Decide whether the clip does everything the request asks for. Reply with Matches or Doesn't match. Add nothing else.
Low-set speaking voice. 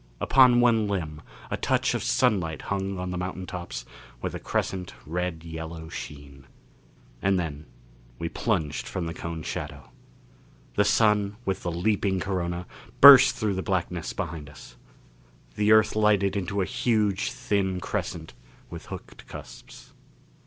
Matches